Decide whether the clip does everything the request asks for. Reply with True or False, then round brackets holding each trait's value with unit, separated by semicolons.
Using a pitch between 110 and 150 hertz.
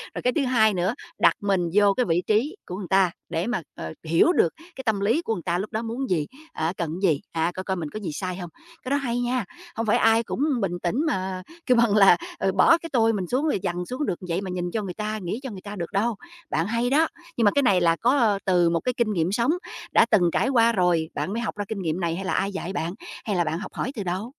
False (200 Hz)